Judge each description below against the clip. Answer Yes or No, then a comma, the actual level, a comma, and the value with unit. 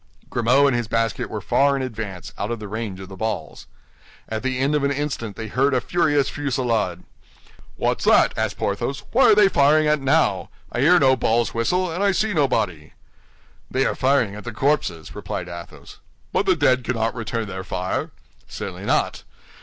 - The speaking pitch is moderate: No, low, 125 Hz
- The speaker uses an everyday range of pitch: Yes, average, 4.9 semitones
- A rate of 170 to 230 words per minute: Yes, average, 190 wpm